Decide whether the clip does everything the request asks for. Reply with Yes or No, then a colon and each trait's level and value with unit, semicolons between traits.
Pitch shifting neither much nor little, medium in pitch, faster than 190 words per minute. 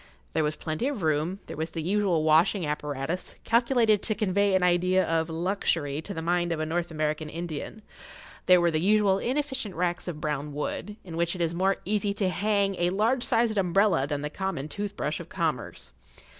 Yes: average, 4.3 semitones; medium, 175 Hz; average, 200 wpm